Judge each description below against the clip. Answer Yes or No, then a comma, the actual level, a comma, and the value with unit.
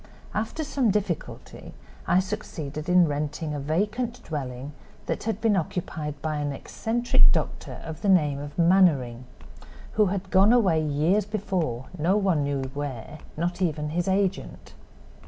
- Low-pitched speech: No, medium, 170 Hz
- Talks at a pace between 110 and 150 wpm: Yes, average, 145 wpm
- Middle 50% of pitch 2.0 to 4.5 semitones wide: No, average, 5.1 semitones